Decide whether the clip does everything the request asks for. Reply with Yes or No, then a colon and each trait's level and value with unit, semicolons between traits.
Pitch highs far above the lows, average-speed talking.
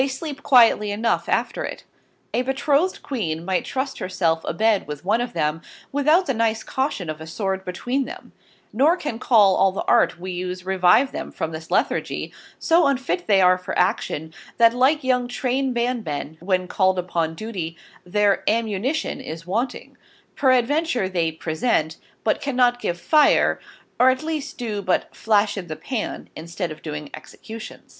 Yes: wide, 6.4 semitones; average, 170 wpm